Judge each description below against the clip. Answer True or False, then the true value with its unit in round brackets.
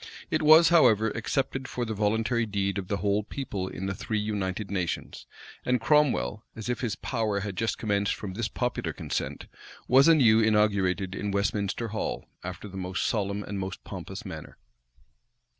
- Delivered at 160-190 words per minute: True (170 wpm)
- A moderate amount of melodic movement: True (3.0 semitones)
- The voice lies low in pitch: True (105 Hz)